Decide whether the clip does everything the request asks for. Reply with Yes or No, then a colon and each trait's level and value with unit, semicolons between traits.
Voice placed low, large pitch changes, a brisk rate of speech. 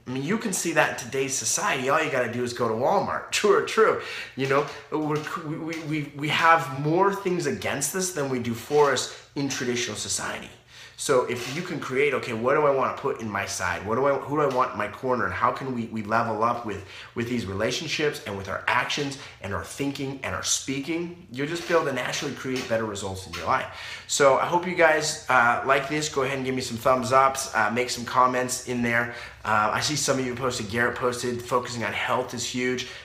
No: low, 130 Hz; average, 3.9 semitones; fast, 240 wpm